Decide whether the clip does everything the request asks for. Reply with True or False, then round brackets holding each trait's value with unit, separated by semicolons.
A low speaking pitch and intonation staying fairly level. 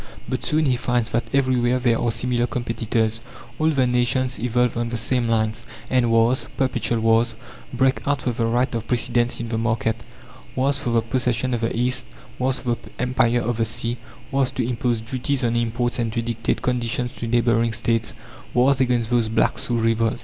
True (120 Hz; 1.7 semitones)